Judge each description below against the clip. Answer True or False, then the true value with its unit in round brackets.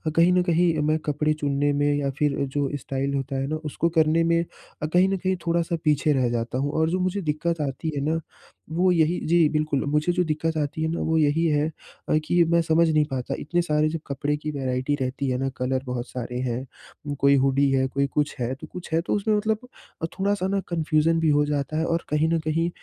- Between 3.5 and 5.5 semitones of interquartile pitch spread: False (3.1 semitones)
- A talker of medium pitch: True (155 Hz)